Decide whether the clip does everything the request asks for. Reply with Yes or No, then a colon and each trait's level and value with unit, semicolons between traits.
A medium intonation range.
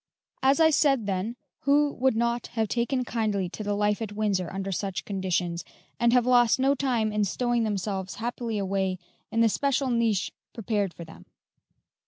Yes: average, 3.7 semitones